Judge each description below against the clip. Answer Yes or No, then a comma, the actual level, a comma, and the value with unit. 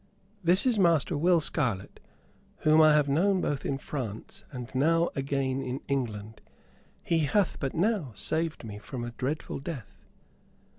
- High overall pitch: No, medium, 140 Hz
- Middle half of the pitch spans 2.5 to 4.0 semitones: No, average, 4.6 semitones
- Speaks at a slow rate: No, average, 150 wpm